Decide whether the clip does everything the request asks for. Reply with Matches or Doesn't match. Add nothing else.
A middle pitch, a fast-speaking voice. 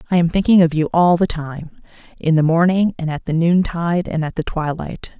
Matches